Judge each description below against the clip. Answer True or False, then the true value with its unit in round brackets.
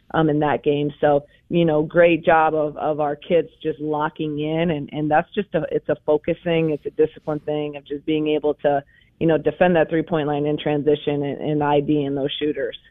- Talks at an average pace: False (225 wpm)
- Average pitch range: False (1.4 semitones)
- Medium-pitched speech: True (150 Hz)